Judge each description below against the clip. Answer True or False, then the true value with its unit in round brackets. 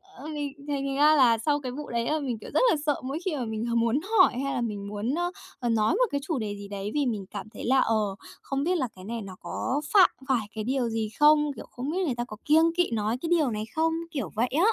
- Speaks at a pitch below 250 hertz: False (255 Hz)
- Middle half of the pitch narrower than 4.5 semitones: False (5.1 semitones)